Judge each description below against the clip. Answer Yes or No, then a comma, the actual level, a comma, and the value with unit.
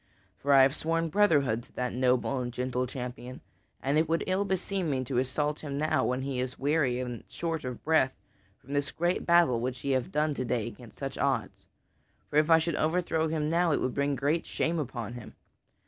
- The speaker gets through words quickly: Yes, fast, 210 wpm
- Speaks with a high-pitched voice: No, medium, 140 Hz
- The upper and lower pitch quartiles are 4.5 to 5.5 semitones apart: No, average, 4.1 semitones